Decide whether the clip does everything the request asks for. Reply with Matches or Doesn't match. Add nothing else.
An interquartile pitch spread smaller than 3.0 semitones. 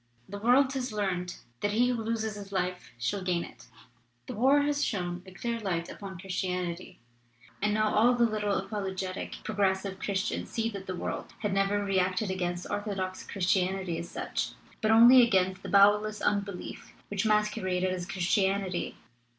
Matches